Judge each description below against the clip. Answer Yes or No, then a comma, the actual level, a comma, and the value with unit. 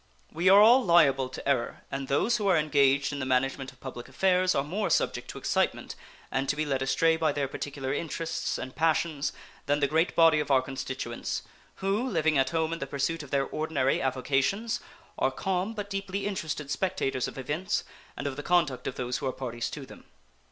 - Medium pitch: Yes, medium, 145 Hz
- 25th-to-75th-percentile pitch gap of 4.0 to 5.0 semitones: Yes, average, 4.3 semitones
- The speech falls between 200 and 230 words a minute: Yes, fast, 205 wpm